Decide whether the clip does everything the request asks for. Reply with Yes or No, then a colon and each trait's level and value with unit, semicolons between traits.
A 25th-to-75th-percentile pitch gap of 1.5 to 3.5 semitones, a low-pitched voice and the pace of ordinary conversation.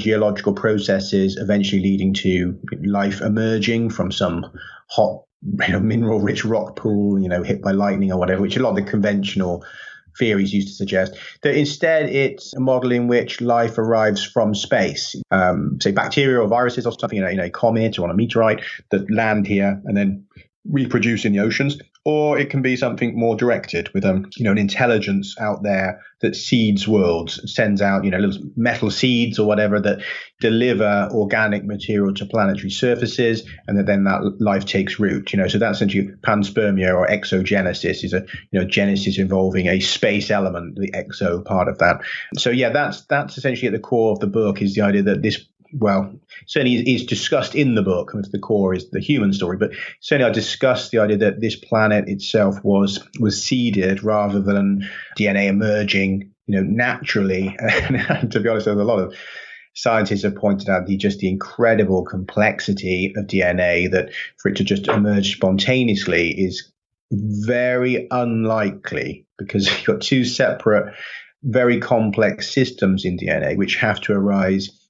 Yes: average, 2.8 semitones; low, 105 Hz; average, 180 wpm